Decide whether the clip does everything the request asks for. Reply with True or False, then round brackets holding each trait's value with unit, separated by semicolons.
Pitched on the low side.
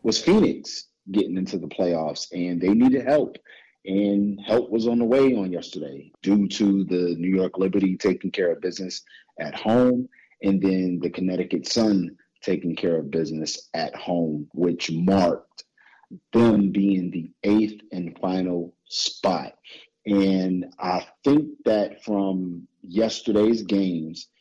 True (95 Hz)